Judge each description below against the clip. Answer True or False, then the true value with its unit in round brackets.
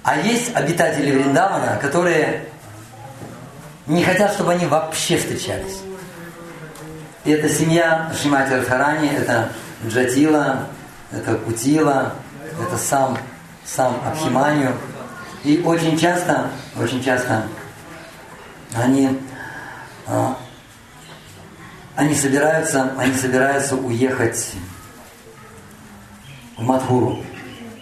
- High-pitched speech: False (135 Hz)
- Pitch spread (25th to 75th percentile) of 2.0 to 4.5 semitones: True (3.9 semitones)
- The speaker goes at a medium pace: False (80 wpm)